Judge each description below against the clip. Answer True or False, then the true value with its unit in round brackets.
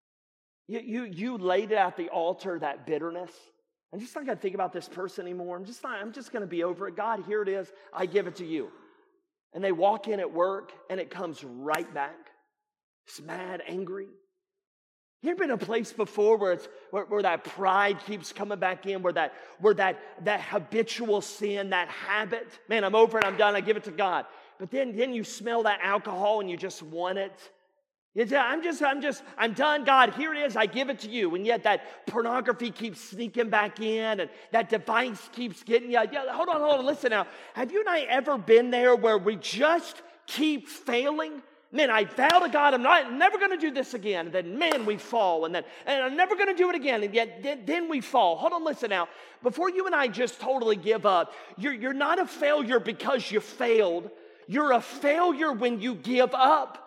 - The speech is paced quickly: True (220 wpm)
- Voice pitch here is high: True (230 Hz)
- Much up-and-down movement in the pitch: True (6.1 semitones)